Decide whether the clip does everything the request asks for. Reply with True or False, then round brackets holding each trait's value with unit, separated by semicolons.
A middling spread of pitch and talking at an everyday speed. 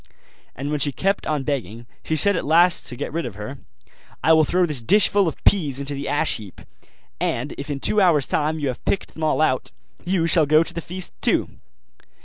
False (3.5 semitones; 220 wpm)